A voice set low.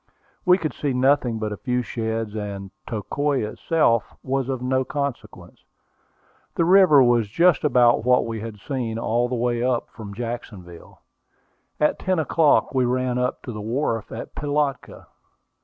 Yes: low, 125 Hz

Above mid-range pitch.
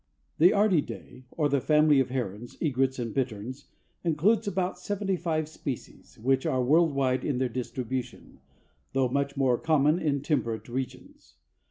No: low, 135 Hz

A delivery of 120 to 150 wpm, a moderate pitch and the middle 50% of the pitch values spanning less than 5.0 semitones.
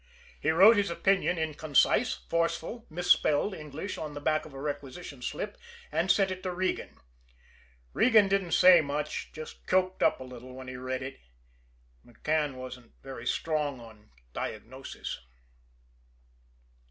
No: average, 140 wpm; medium, 155 Hz; wide, 5.6 semitones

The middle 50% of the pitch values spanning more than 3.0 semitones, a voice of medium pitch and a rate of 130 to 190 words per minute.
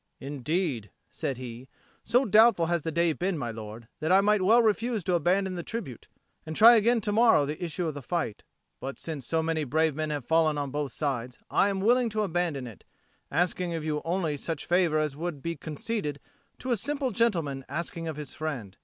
No: average, 5.1 semitones; medium, 165 Hz; fast, 205 wpm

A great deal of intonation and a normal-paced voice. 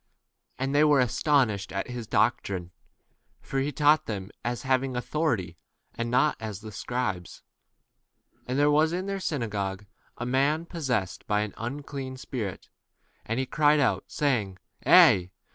Yes: wide, 5.7 semitones; average, 160 wpm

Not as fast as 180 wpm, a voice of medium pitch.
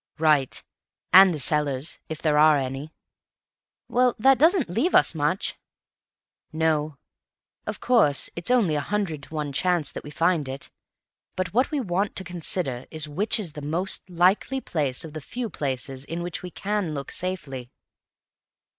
Yes: average, 165 wpm; medium, 160 Hz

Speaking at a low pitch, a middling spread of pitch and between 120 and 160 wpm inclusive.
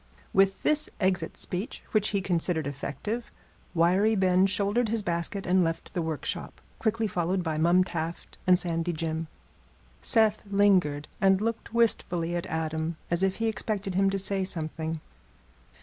No: medium, 185 Hz; average, 3.5 semitones; average, 150 wpm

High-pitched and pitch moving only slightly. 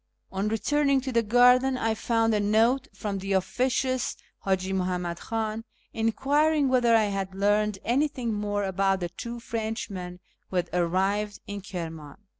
No: high, 210 Hz; average, 4.0 semitones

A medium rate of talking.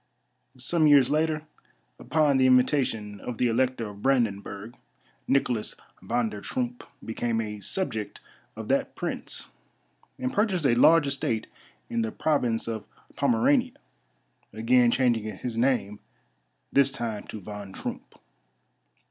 No: slow, 125 wpm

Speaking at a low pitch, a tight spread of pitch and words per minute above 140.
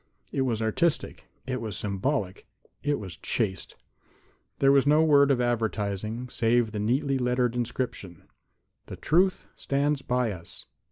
No: low, 125 Hz; average, 4.2 semitones; average, 160 wpm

